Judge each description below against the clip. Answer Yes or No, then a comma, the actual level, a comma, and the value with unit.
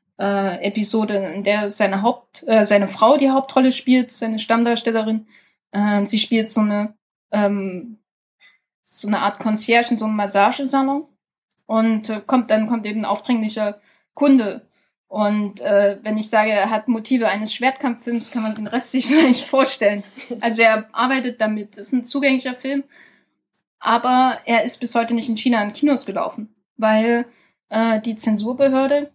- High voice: Yes, high, 225 Hz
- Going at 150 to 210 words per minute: Yes, average, 160 wpm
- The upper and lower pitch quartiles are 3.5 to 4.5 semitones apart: No, average, 3.1 semitones